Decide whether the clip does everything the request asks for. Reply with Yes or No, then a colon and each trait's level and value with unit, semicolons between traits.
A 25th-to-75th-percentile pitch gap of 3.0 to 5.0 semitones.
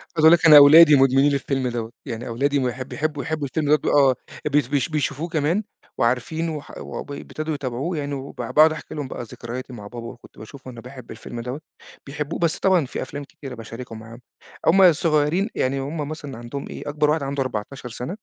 Yes: average, 3.5 semitones